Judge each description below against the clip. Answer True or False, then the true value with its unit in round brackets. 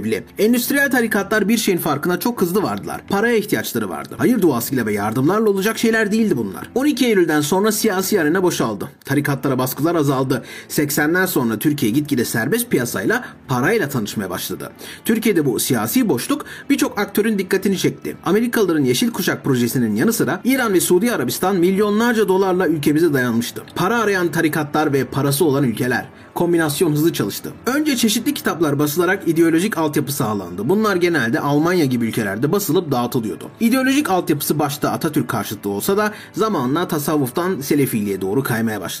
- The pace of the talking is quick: True (150 wpm)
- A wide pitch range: True (7.1 semitones)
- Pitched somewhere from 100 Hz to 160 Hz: False (175 Hz)